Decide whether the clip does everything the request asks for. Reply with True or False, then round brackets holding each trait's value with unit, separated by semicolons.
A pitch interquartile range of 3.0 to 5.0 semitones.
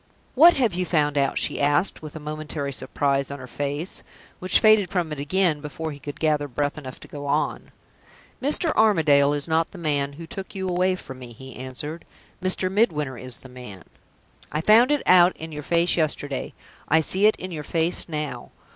True (4.3 semitones)